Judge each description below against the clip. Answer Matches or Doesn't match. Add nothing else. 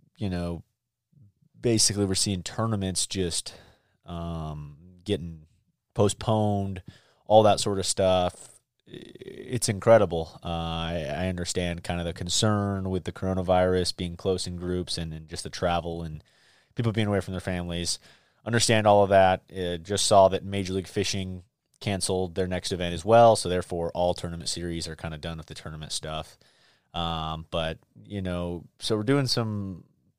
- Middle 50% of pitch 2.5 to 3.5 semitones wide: Matches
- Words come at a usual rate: Matches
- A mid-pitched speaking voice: Doesn't match